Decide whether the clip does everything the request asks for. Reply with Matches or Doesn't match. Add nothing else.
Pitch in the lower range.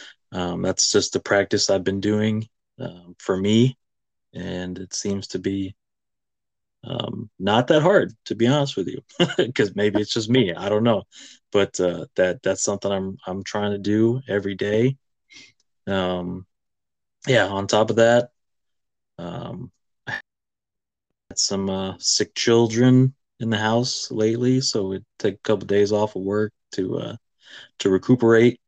Matches